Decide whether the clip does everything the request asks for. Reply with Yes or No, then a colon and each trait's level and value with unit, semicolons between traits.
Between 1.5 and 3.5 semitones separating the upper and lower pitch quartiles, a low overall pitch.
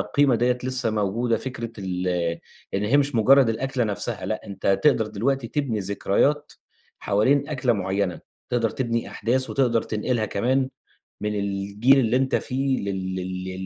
No: average, 4.7 semitones; low, 115 Hz